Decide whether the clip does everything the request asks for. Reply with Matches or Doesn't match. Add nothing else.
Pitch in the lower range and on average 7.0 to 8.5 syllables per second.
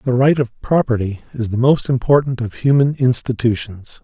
Doesn't match